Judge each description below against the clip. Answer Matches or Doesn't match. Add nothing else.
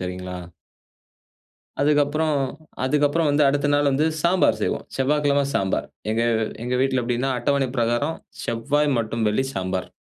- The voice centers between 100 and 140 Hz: Matches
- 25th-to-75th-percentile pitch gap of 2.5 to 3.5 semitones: Doesn't match